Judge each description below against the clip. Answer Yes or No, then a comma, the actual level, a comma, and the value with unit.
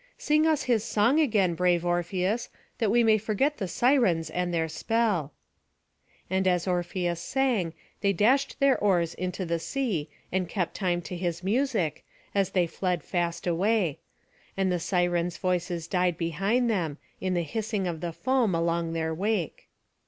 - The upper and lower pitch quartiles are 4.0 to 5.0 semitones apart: Yes, average, 4.3 semitones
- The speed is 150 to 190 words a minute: Yes, average, 160 wpm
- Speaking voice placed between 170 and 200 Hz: Yes, medium, 185 Hz